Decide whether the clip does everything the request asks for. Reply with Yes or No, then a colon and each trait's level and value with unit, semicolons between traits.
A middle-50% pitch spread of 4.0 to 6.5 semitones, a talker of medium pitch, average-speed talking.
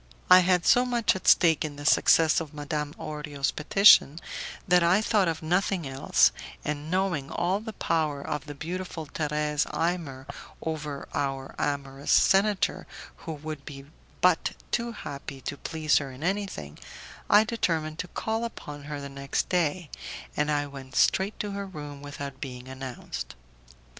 Yes: average, 4.3 semitones; medium, 155 Hz; average, 160 wpm